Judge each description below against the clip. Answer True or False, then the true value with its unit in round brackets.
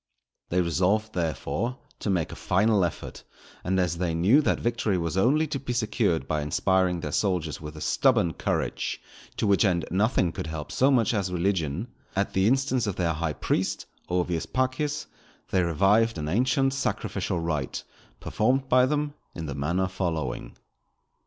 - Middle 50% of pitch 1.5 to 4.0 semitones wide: False (5.6 semitones)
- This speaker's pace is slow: False (170 wpm)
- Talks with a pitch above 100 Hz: False (95 Hz)